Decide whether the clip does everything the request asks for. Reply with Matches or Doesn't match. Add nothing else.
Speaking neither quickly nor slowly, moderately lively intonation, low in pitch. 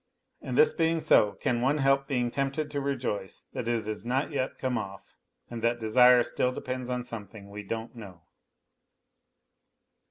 Matches